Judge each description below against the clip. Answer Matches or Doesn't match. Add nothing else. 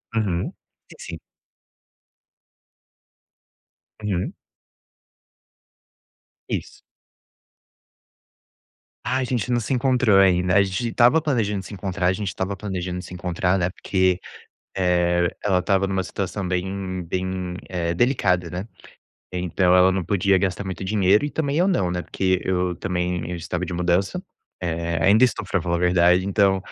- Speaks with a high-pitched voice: Doesn't match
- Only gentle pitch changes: Matches